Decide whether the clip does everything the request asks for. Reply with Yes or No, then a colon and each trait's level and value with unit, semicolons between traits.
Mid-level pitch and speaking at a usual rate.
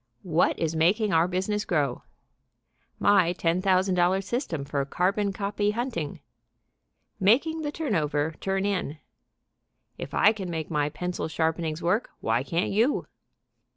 No: medium, 180 Hz; slow, 130 wpm